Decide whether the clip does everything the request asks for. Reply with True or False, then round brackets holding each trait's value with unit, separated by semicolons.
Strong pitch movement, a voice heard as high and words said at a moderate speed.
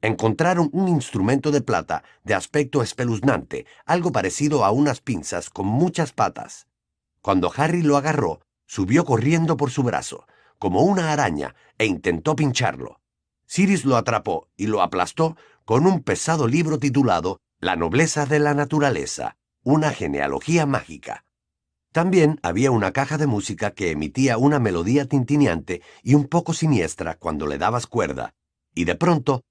False (5.7 semitones; 140 Hz; 145 wpm)